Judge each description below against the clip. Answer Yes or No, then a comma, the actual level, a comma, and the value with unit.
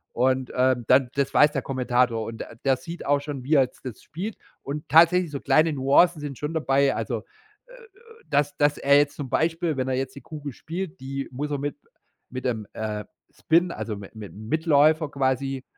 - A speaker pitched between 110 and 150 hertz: Yes, medium, 140 Hz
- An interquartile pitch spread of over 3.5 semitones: No, average, 3.2 semitones